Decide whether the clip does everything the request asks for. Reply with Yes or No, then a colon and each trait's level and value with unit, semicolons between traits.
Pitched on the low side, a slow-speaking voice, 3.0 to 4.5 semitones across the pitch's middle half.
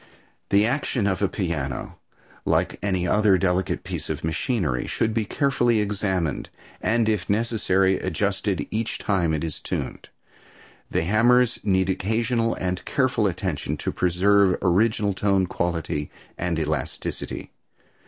Yes: very low, 95 Hz; slow, 130 wpm; average, 3.6 semitones